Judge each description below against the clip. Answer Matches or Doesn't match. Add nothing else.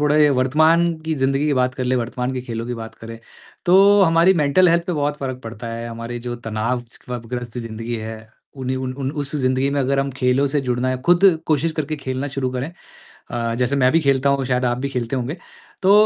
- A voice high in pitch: Doesn't match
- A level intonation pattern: Doesn't match